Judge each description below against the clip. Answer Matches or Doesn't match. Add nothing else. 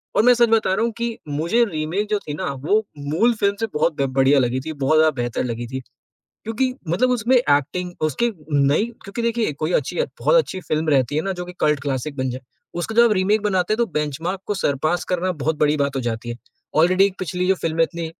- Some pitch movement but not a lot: Doesn't match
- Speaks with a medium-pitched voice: Matches